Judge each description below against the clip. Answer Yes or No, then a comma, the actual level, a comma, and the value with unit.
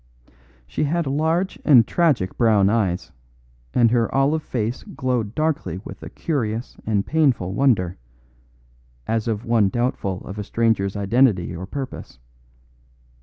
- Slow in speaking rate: Yes, slow, 130 wpm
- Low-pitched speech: Yes, low, 115 Hz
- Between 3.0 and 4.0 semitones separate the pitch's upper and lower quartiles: No, wide, 5.4 semitones